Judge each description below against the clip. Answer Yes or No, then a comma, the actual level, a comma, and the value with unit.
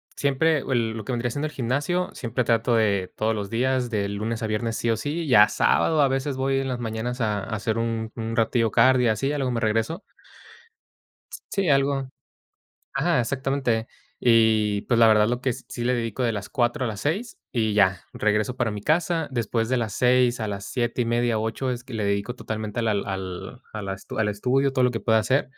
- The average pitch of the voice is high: No, low, 120 Hz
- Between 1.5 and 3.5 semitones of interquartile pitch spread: Yes, average, 3.2 semitones